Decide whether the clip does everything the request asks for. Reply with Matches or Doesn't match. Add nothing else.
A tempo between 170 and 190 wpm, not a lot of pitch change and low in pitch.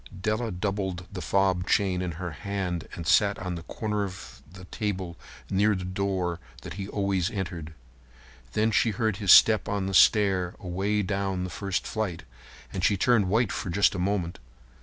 Matches